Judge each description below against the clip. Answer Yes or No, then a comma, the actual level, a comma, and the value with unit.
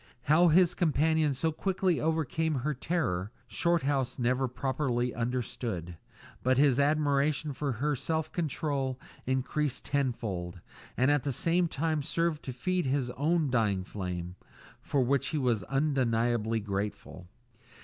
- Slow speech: Yes, slow, 130 wpm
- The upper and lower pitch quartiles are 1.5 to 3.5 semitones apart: No, average, 4.2 semitones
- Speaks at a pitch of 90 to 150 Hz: Yes, low, 135 Hz